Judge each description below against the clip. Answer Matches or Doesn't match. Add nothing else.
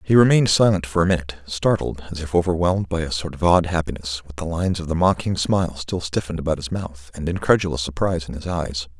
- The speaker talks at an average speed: Doesn't match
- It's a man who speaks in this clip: Matches